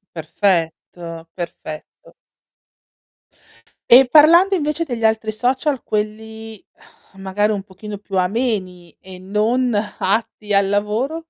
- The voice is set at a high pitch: Yes, high, 210 Hz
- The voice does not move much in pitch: No, average, 4.3 semitones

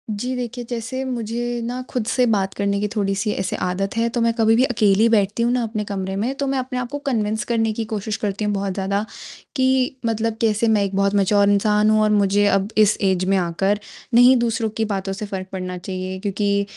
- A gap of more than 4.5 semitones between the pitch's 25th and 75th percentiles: No, average, 2.8 semitones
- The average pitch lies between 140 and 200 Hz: No, high, 210 Hz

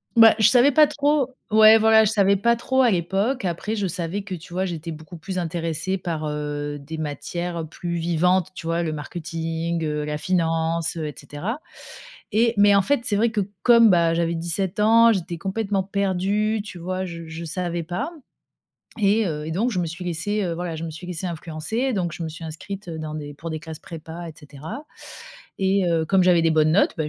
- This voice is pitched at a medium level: Yes, medium, 175 Hz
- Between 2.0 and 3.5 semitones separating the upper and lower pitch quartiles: No, average, 4.0 semitones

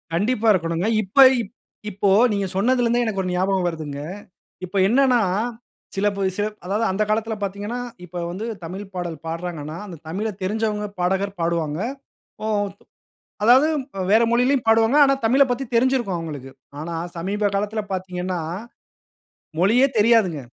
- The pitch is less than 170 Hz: No, high, 200 Hz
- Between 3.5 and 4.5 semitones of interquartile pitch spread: Yes, average, 4.2 semitones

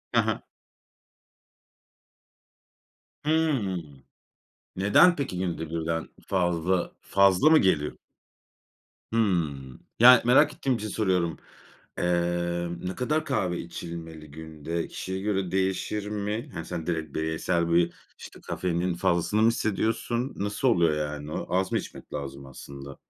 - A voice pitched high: No, very low, 90 Hz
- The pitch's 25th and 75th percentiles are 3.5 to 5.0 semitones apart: Yes, average, 4.4 semitones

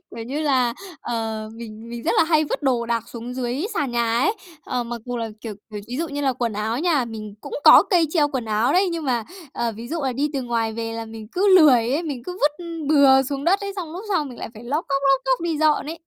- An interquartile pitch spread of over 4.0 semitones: Yes, average, 4.7 semitones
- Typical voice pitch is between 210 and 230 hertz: No, very high, 255 Hz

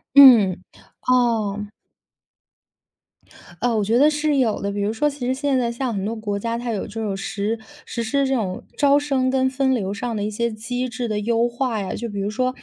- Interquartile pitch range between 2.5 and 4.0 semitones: Yes, average, 3.6 semitones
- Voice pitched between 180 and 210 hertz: No, high, 235 Hz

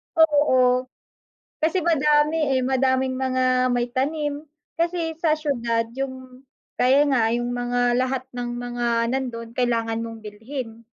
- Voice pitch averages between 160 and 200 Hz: No, very high, 255 Hz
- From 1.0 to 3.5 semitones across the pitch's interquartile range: Yes, average, 3.1 semitones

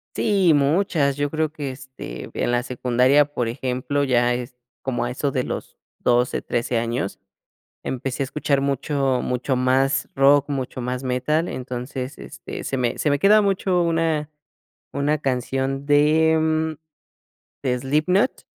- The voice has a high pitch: No, low, 135 Hz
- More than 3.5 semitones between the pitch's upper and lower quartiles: No, average, 3.2 semitones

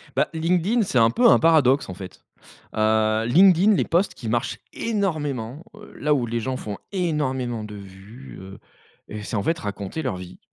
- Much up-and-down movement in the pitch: Yes, wide, 7.3 semitones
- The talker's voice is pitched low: Yes, low, 130 Hz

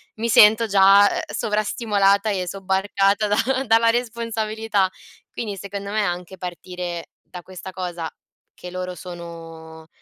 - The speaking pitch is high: Yes, high, 195 Hz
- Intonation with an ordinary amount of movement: Yes, average, 3.1 semitones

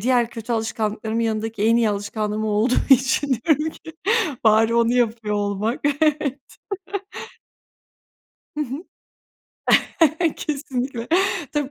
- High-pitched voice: Yes, high, 230 Hz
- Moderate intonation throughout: Yes, average, 3.5 semitones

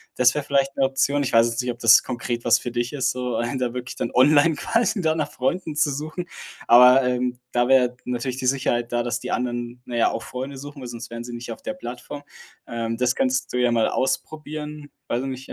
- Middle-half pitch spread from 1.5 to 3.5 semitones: Yes, average, 2.7 semitones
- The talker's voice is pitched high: No, low, 125 Hz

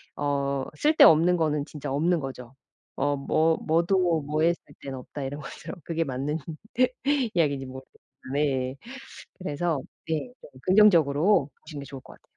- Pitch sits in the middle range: Yes, medium, 150 Hz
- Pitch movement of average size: Yes, average, 3.3 semitones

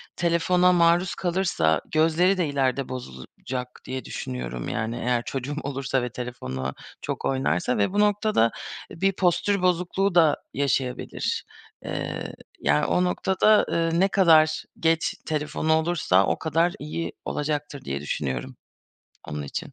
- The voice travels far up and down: Yes, wide, 6.0 semitones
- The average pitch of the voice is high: No, medium, 150 Hz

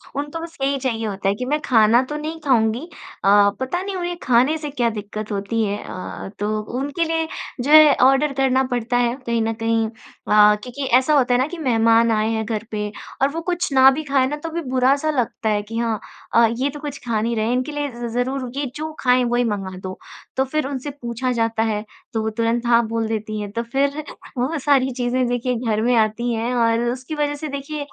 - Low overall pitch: No, high, 245 Hz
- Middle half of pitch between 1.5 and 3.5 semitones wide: No, average, 4.0 semitones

